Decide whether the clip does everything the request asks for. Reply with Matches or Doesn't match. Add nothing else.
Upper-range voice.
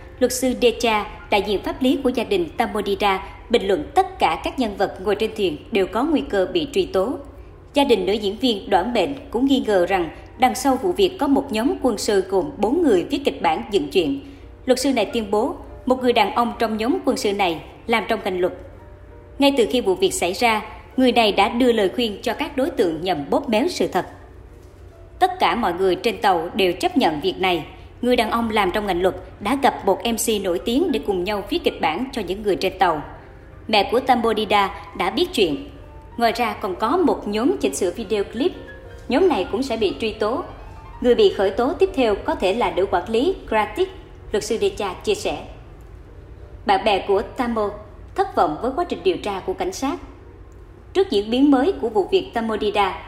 Matches